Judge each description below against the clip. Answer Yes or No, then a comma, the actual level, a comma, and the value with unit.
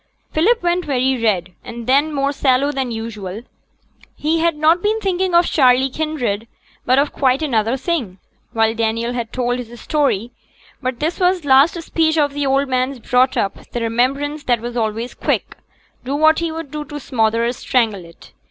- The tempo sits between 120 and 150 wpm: No, average, 175 wpm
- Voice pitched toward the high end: Yes, very high, 265 Hz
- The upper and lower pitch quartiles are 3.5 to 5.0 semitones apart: Yes, average, 4.6 semitones